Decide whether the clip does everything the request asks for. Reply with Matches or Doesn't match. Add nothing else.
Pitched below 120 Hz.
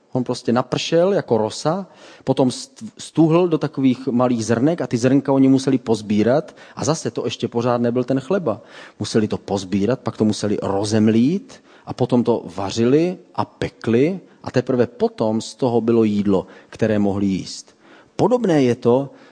Doesn't match